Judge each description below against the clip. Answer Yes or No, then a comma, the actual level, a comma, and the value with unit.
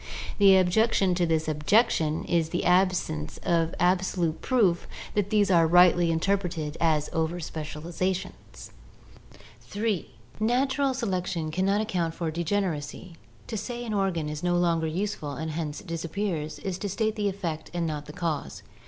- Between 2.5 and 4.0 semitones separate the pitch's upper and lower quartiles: Yes, average, 3.7 semitones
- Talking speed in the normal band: Yes, average, 155 wpm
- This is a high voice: No, medium, 175 Hz